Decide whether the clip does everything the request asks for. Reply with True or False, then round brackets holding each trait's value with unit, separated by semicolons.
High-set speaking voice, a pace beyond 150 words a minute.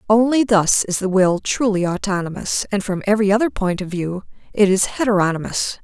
True (200 Hz; 175 wpm)